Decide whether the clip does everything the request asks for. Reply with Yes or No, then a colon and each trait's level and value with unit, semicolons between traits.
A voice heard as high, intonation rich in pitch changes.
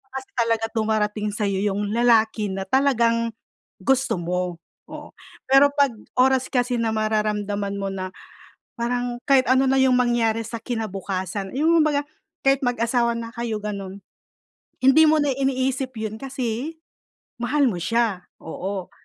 No: high, 230 Hz; average, 3.9 semitones